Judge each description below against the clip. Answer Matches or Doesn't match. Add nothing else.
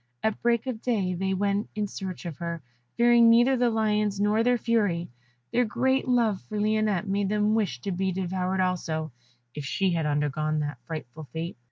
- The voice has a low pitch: Doesn't match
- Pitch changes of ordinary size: Matches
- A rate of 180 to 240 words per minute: Matches